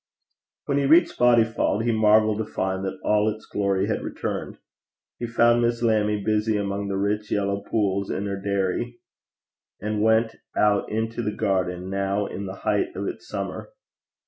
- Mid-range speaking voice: No, low, 105 Hz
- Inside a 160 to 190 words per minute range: Yes, average, 170 wpm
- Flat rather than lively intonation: Yes, narrow, 2.2 semitones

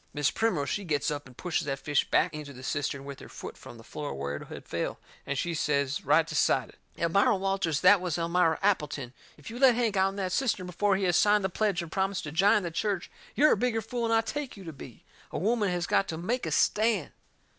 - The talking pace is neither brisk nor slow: No, fast, 240 wpm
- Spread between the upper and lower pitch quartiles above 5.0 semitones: Yes, wide, 5.6 semitones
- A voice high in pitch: No, medium, 180 Hz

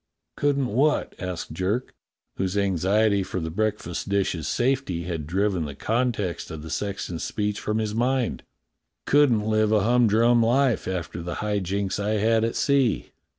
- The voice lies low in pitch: Yes, low, 105 Hz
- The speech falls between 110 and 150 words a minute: No, average, 160 wpm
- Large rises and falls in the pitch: No, average, 4.1 semitones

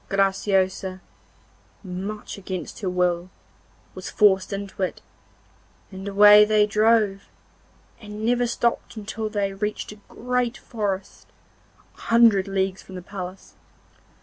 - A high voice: Yes, high, 200 Hz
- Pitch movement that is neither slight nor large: No, narrow, 2.0 semitones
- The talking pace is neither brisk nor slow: No, slow, 120 wpm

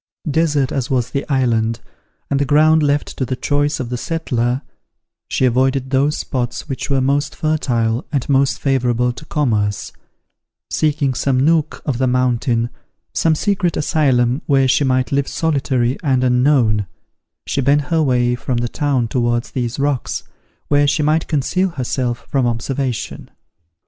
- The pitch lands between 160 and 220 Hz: No, low, 135 Hz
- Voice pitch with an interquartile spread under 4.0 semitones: Yes, average, 2.9 semitones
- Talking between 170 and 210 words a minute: No, average, 155 wpm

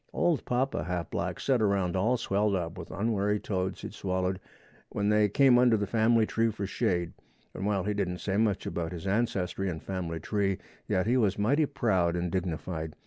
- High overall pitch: No, low, 100 Hz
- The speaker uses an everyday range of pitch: Yes, average, 3.3 semitones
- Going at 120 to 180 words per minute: No, average, 195 wpm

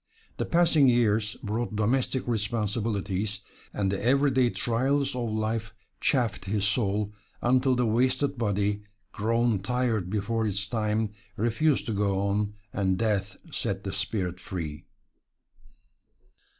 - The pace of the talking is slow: Yes, slow, 125 wpm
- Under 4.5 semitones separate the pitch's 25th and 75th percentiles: Yes, average, 3.1 semitones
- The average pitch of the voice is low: Yes, low, 110 Hz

